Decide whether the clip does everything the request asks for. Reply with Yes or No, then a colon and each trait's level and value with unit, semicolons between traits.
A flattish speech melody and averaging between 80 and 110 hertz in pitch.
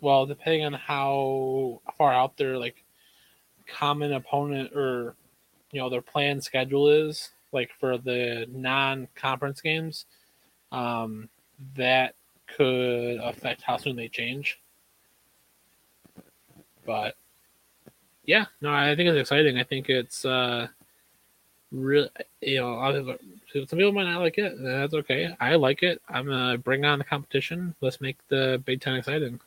No: narrow, 2.3 semitones; low, 135 Hz